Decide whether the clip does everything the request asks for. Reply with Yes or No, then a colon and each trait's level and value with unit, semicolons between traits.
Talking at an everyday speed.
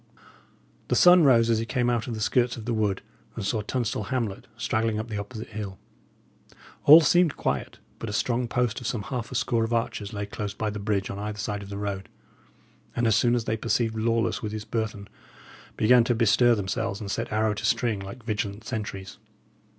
No: fast, 210 wpm